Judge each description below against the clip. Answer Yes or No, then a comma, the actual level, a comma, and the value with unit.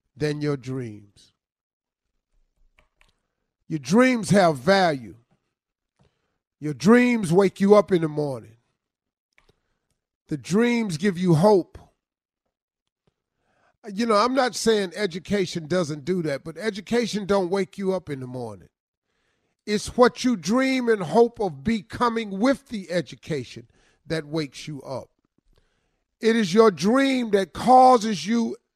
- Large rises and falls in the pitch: Yes, wide, 7.1 semitones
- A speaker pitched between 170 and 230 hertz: Yes, high, 190 Hz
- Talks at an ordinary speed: No, slow, 125 wpm